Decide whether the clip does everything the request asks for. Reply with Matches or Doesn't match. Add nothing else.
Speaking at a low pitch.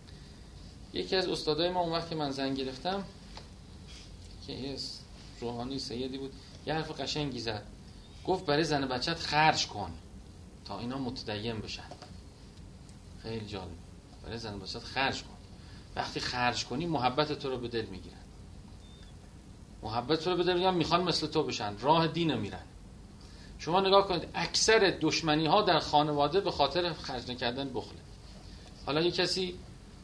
Matches